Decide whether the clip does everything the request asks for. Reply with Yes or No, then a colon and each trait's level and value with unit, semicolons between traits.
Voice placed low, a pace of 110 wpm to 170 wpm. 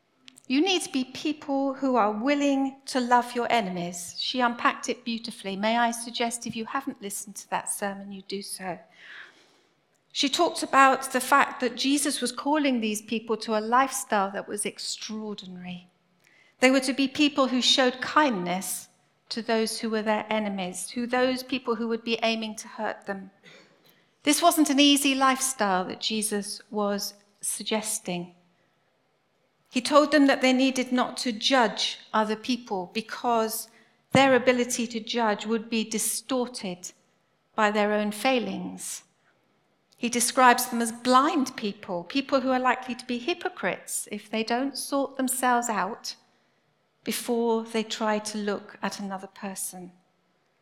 No: high, 235 Hz; average, 155 wpm